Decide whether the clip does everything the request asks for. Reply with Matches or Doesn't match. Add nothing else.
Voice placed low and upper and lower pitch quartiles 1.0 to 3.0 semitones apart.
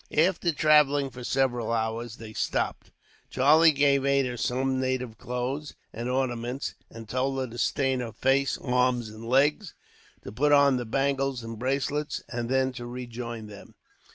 Matches